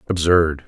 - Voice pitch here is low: Yes, very low, 85 Hz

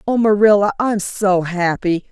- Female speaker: Yes, female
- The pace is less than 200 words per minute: Yes, average, 140 wpm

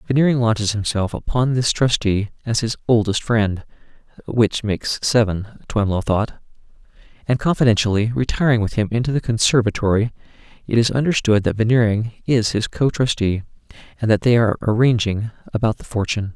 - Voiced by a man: Yes, male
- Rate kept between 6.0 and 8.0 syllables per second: No, 4.9 syllables/s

